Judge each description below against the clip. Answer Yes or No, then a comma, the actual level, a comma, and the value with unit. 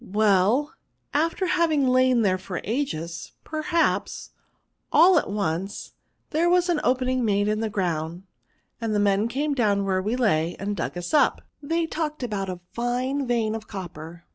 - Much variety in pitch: Yes, wide, 6.9 semitones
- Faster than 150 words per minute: Yes, average, 165 wpm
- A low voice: No, high, 225 Hz